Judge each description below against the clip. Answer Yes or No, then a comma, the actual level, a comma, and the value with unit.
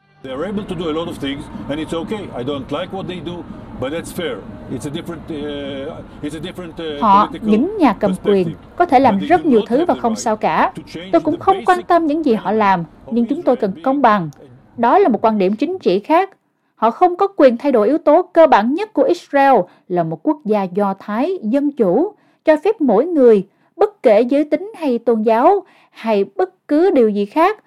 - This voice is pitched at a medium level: No, high, 230 Hz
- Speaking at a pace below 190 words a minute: Yes, slow, 165 wpm